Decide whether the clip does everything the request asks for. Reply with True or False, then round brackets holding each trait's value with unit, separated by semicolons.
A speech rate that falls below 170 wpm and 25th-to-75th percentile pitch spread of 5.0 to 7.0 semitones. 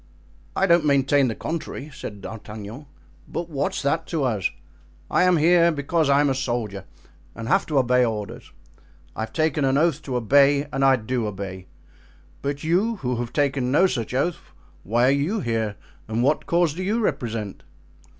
False (175 wpm; 5.5 semitones)